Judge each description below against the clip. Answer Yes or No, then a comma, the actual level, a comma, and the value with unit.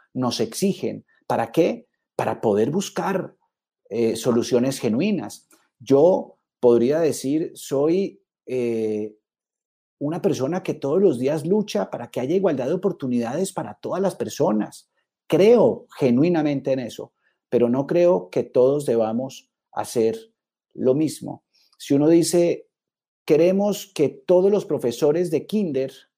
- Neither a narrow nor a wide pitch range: No, wide, 6.9 semitones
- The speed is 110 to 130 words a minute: Yes, slow, 125 wpm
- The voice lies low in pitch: No, medium, 165 Hz